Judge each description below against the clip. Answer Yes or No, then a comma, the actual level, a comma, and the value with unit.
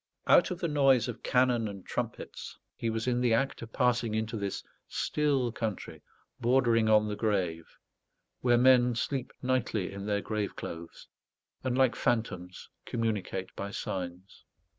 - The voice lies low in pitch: Yes, low, 115 Hz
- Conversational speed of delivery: Yes, average, 150 wpm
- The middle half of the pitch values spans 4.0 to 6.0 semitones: No, average, 3.6 semitones